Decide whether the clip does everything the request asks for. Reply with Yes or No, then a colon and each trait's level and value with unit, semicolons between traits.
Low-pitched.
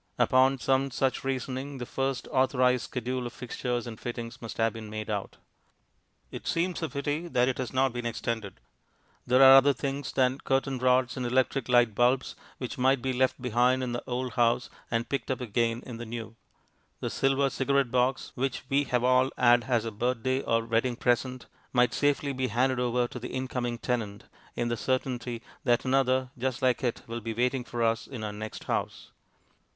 Yes: low, 125 Hz